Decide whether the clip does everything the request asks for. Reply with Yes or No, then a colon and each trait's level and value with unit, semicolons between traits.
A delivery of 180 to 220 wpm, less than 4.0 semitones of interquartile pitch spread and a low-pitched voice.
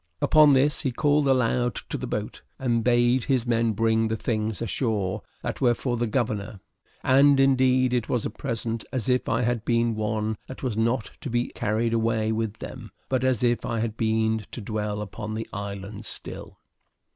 Yes: average, 190 wpm; narrow, 2.6 semitones; low, 115 Hz